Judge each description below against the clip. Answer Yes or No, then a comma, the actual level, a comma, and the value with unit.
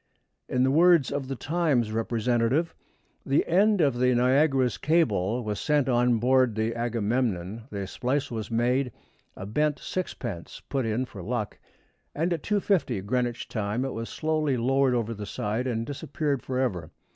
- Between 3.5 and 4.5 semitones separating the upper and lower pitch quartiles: Yes, average, 3.9 semitones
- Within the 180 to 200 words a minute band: No, average, 155 wpm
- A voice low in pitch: Yes, low, 125 Hz